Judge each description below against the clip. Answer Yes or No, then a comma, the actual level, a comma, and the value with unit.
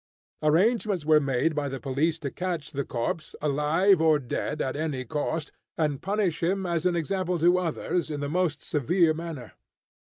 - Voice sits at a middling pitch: Yes, medium, 160 Hz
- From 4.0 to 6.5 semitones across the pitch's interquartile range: No, average, 3.3 semitones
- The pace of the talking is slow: No, average, 170 wpm